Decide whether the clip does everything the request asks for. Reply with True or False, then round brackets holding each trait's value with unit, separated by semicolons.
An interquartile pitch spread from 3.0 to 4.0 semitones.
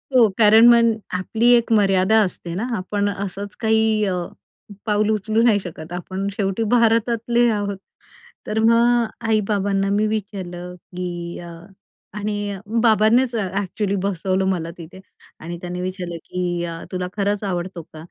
True (3.3 semitones)